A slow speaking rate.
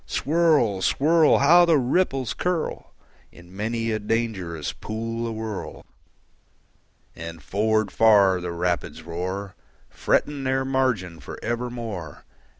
Yes: slow, 110 wpm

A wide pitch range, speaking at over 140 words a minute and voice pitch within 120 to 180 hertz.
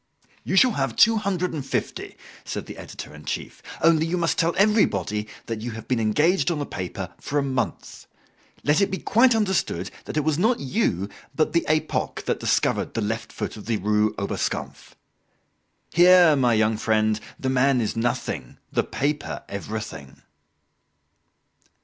Yes: wide, 8.0 semitones; average, 170 wpm; low, 135 Hz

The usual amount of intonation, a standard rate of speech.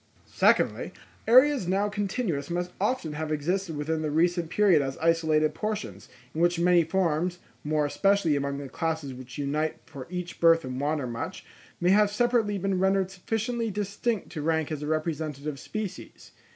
Yes: average, 4.7 semitones; average, 160 wpm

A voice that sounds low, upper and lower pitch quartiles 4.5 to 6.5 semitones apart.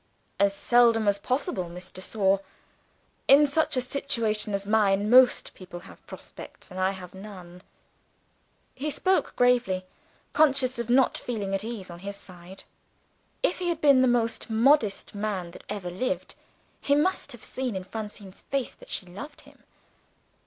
No: high, 215 Hz; average, 5.0 semitones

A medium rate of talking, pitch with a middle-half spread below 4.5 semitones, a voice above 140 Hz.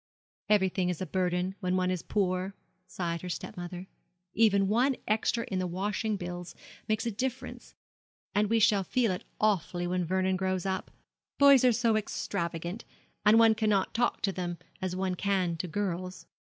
Yes: average, 165 wpm; average, 3.0 semitones; high, 190 Hz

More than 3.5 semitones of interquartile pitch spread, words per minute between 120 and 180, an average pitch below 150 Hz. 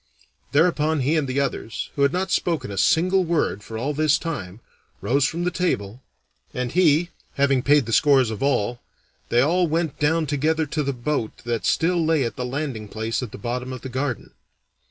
No: average, 4.6 semitones; average, 195 wpm; medium, 140 Hz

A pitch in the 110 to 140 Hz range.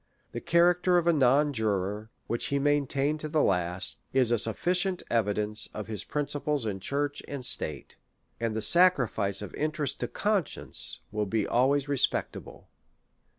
Yes: low, 135 Hz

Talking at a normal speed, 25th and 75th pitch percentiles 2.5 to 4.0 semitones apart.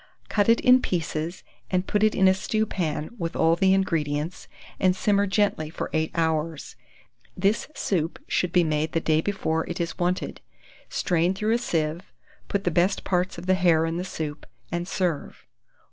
Yes: average, 175 wpm; average, 3.0 semitones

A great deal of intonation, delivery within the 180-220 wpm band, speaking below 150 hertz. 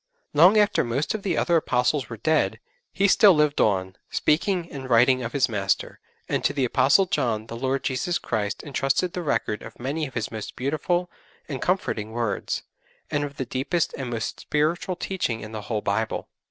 Yes: wide, 6.3 semitones; average, 190 wpm; low, 135 Hz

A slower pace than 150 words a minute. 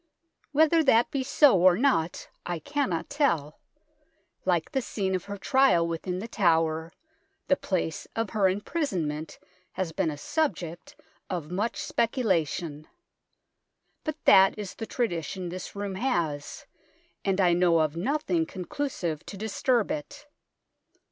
Yes: slow, 135 wpm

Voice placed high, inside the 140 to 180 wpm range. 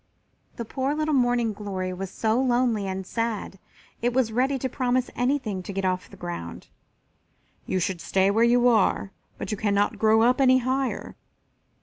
Yes: high, 230 Hz; average, 175 wpm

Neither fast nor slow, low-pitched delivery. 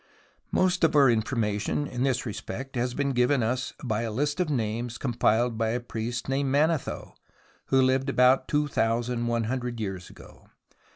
Yes: average, 170 wpm; low, 125 Hz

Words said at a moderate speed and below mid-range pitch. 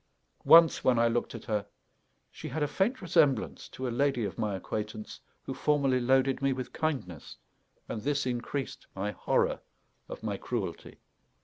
Yes: average, 165 wpm; low, 130 Hz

